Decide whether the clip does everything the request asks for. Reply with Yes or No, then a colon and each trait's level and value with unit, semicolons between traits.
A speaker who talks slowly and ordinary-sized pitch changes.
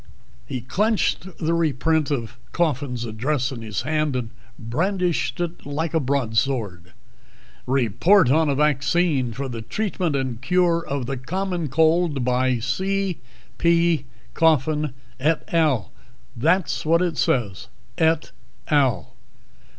Yes: slow, 125 wpm; average, 5.0 semitones